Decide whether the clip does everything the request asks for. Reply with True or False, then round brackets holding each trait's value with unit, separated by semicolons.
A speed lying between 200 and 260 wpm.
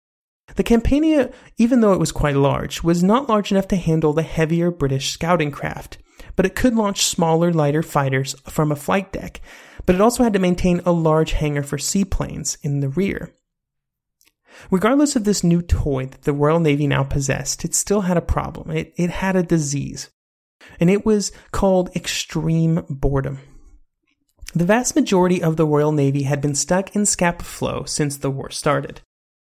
False (180 wpm)